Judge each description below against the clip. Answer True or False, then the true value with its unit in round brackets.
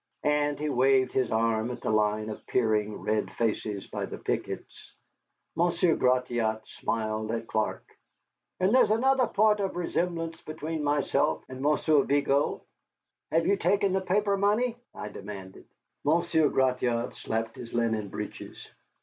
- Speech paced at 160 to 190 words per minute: False (140 wpm)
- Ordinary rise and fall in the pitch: False (7.4 semitones)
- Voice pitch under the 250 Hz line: True (135 Hz)